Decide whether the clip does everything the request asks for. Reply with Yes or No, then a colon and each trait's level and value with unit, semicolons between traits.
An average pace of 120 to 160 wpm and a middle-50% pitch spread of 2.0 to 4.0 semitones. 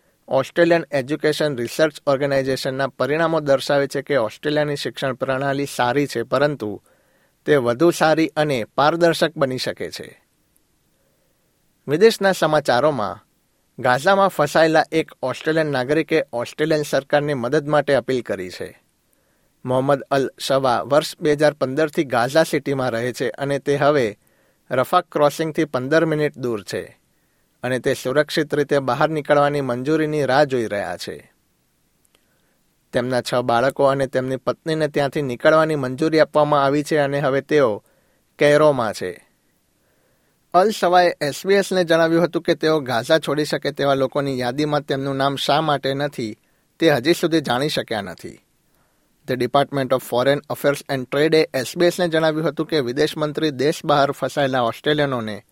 Yes: average, 135 wpm; average, 2.8 semitones